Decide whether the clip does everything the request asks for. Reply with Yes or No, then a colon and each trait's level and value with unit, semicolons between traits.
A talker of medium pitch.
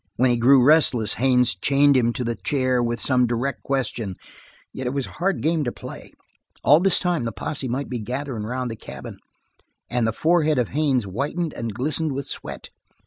No: low, 130 Hz